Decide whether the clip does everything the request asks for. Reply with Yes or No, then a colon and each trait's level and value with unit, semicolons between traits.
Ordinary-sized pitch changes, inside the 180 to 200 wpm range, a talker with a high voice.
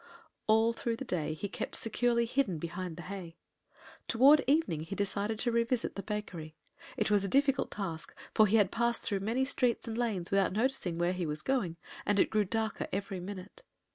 Yes: average, 4.4 semitones; average, 195 wpm; high, 205 Hz